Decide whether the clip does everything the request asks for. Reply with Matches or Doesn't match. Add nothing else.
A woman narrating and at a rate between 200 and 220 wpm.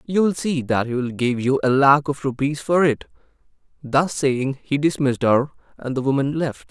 Doesn't match